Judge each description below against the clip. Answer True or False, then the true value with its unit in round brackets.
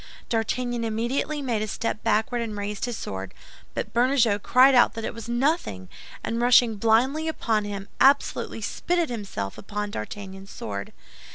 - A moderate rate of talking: True (155 wpm)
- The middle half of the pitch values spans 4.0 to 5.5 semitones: False (3.3 semitones)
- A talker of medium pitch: False (225 Hz)